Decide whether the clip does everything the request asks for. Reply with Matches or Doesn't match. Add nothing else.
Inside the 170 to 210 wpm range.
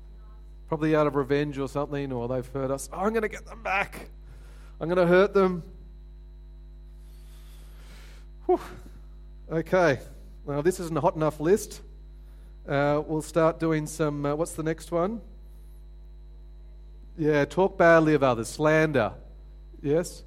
Doesn't match